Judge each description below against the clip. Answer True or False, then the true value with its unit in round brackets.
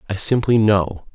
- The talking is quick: False (155 wpm)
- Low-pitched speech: True (105 Hz)